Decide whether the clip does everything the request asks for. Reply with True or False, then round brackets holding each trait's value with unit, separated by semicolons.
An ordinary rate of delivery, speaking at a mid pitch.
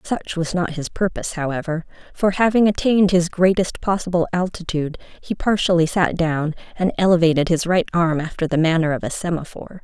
True (170 wpm; 170 Hz)